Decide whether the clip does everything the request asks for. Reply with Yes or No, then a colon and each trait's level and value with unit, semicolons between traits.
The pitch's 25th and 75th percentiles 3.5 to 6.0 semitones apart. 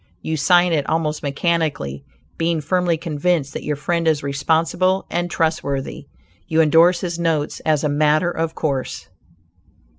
No: narrow, 2.6 semitones